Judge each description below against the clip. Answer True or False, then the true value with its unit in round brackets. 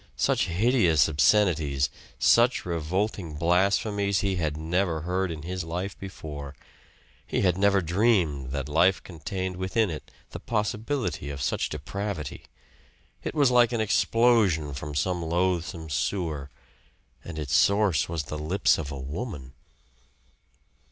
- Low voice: True (90 Hz)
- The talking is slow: True (130 wpm)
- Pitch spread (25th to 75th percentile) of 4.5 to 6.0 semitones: True (4.8 semitones)